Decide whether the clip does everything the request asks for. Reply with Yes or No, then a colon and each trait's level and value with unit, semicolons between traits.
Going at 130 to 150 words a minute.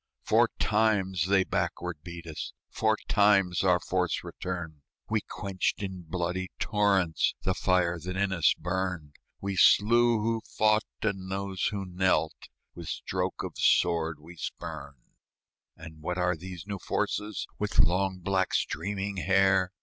Yes: average, 140 wpm